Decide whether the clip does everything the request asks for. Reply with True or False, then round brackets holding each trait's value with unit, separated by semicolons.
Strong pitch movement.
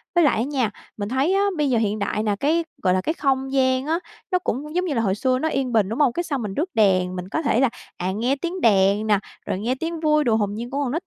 True (6.2 semitones)